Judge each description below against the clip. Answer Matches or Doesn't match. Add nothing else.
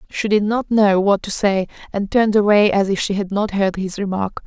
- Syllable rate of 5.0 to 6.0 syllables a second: Matches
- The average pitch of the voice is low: Doesn't match